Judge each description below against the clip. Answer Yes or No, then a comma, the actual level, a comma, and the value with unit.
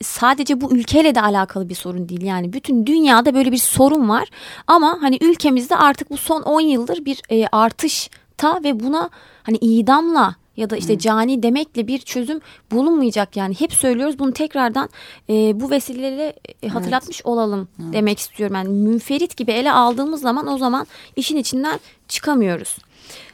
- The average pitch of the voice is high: Yes, very high, 255 Hz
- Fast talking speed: Yes, fast, 150 wpm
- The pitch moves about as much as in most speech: Yes, average, 4.8 semitones